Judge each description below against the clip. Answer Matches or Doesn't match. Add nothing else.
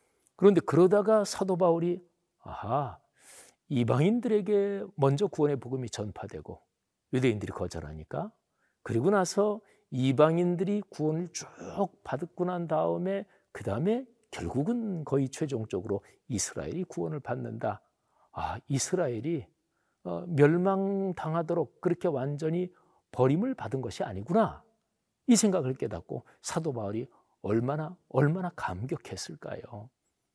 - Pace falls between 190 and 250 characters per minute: Doesn't match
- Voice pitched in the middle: Matches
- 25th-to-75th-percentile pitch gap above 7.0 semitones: Doesn't match